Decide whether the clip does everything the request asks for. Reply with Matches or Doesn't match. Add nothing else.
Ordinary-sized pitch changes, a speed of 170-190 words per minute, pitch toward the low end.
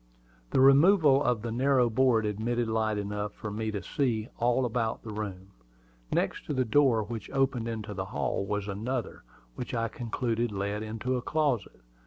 Matches